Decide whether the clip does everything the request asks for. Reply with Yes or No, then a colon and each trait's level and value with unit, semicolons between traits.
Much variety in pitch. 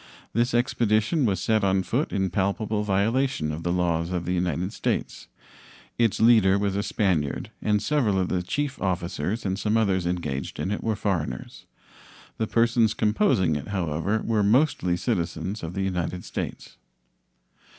No: average, 3.7 semitones